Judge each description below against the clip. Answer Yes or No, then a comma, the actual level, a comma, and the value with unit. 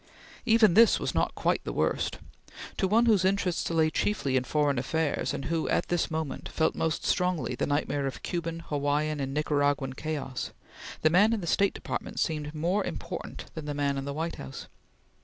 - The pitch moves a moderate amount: Yes, average, 3.5 semitones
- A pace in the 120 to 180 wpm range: No, average, 190 wpm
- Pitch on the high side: No, medium, 155 Hz